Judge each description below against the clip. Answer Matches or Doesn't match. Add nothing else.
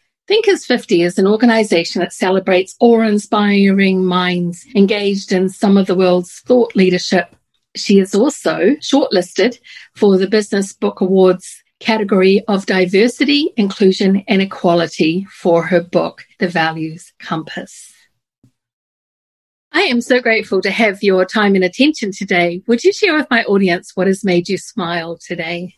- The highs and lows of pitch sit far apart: Doesn't match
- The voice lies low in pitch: Doesn't match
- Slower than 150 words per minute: Matches